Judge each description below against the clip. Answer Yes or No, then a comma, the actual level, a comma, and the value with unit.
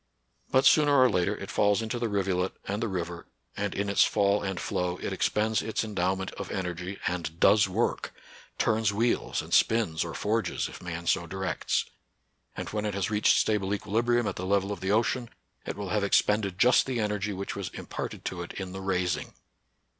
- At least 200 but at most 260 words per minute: Yes, fast, 205 wpm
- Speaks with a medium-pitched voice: No, low, 100 Hz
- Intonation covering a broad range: No, average, 2.8 semitones